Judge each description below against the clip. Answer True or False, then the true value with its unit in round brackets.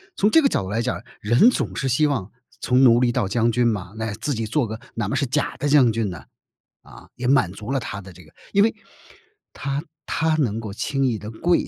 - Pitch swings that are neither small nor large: True (4.7 semitones)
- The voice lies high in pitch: False (120 Hz)